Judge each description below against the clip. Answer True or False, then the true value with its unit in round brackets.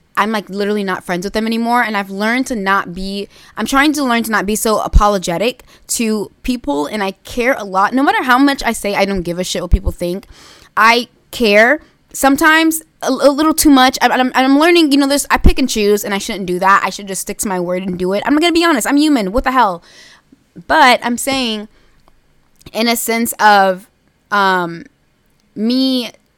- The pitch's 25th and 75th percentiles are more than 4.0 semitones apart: True (4.9 semitones)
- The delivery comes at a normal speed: False (220 wpm)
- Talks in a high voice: True (225 Hz)